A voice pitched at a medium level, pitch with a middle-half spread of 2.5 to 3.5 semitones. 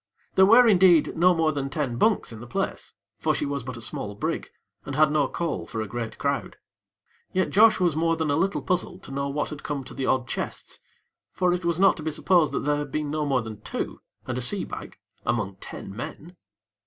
No: medium, 150 Hz; average, 4.8 semitones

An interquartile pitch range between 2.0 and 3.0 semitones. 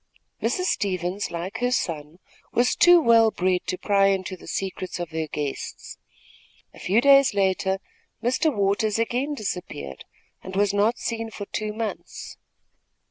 No: average, 4.0 semitones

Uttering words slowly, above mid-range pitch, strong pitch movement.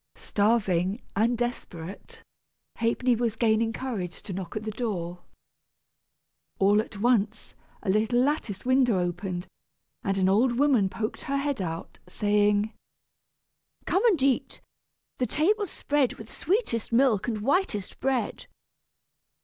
No: slow, 125 wpm; high, 220 Hz; average, 4.3 semitones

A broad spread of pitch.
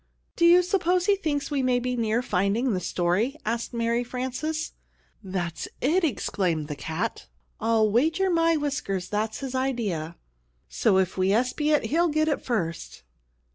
Yes: wide, 7.8 semitones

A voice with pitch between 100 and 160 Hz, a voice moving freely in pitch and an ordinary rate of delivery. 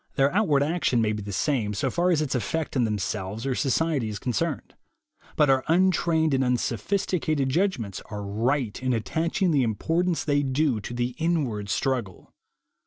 Yes: low, 135 Hz; wide, 6.1 semitones; average, 175 wpm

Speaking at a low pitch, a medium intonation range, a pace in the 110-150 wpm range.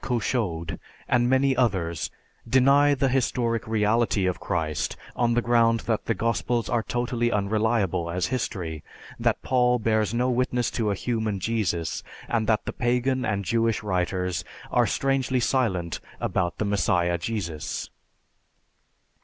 Yes: low, 115 Hz; average, 4.5 semitones; slow, 135 wpm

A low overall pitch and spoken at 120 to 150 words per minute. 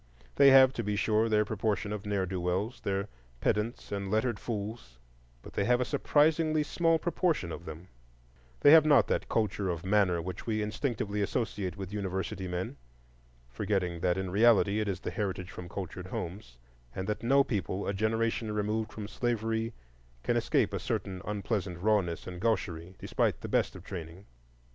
No: low, 105 Hz; average, 175 wpm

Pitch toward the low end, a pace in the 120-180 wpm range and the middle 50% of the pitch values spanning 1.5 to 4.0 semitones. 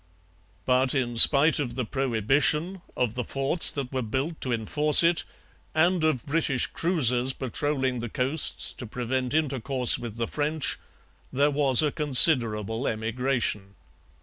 Yes: low, 130 Hz; average, 140 wpm; average, 3.6 semitones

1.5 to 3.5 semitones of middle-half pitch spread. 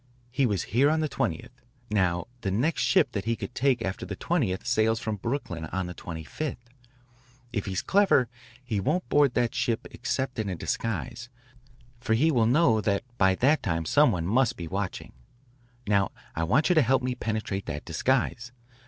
No: wide, 5.5 semitones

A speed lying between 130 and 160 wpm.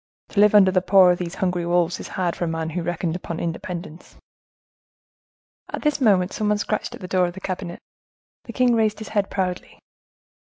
No: average, 200 wpm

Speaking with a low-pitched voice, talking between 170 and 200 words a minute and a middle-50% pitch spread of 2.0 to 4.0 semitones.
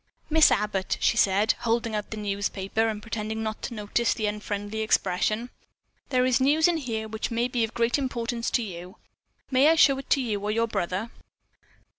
No: high, 220 Hz; average, 180 wpm; narrow, 2.6 semitones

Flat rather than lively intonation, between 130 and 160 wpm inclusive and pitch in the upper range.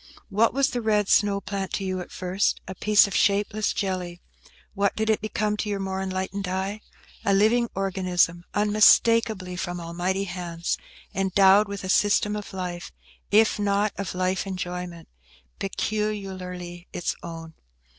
Yes: narrow, 2.3 semitones; average, 150 wpm; high, 195 Hz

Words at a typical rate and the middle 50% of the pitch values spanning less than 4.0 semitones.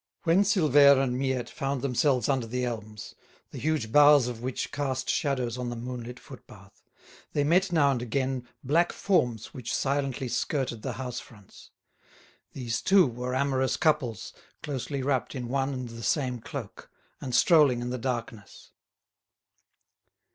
Yes: average, 150 wpm; average, 2.7 semitones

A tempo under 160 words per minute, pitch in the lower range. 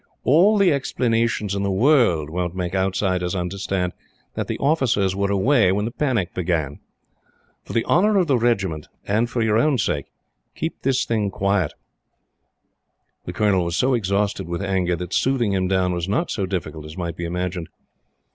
No: average, 175 wpm; low, 100 Hz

